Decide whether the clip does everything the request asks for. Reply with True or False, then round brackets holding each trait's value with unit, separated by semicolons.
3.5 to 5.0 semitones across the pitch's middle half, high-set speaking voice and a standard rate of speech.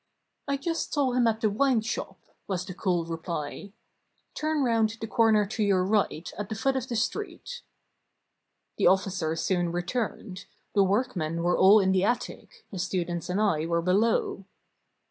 True (4.4 semitones; 200 Hz; 165 wpm)